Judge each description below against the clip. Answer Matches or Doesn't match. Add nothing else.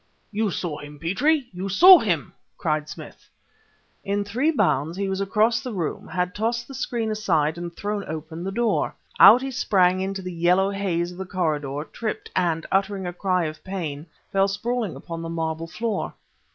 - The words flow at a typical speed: Matches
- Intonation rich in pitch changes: Doesn't match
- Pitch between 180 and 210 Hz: Matches